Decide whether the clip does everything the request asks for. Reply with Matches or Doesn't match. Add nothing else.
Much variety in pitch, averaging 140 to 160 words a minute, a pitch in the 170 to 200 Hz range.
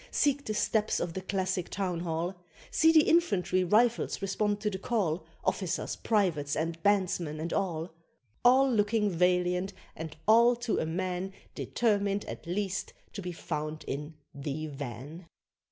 Doesn't match